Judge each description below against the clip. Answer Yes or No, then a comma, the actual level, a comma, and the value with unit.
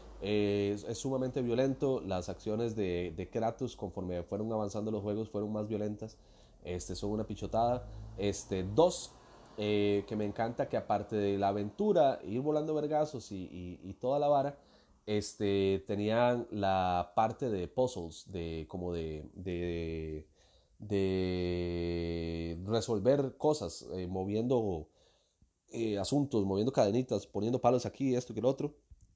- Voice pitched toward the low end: Yes, low, 105 Hz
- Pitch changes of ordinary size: Yes, average, 4.1 semitones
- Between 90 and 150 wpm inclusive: Yes, average, 140 wpm